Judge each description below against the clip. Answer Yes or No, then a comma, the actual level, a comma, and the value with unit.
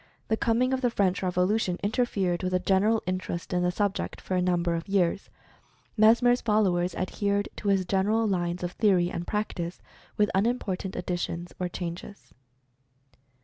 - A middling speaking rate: Yes, average, 155 wpm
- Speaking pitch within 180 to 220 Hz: Yes, high, 190 Hz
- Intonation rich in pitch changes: No, average, 3.0 semitones